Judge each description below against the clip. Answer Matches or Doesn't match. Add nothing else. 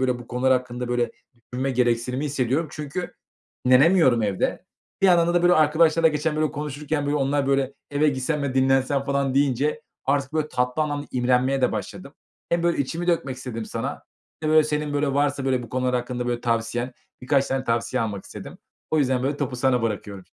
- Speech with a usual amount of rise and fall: Matches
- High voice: Doesn't match